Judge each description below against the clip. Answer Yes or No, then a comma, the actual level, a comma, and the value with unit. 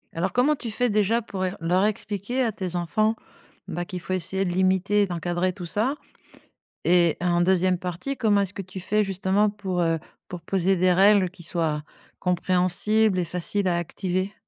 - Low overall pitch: No, medium, 185 Hz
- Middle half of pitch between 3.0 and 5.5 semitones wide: No, narrow, 2.6 semitones